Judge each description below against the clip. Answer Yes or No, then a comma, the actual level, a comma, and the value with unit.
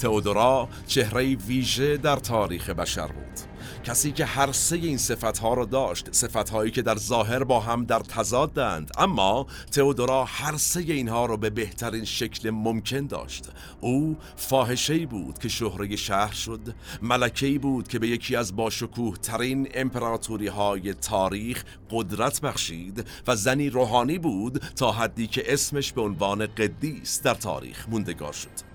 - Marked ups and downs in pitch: No, average, 3.5 semitones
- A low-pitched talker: Yes, low, 115 Hz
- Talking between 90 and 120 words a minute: No, average, 150 wpm